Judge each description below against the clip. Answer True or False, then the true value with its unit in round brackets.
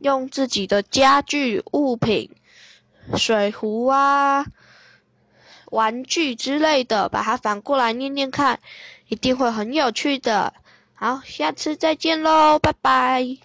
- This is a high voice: True (270 Hz)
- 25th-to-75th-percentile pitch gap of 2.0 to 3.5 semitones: True (3.1 semitones)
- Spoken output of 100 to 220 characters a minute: True (175 characters per minute)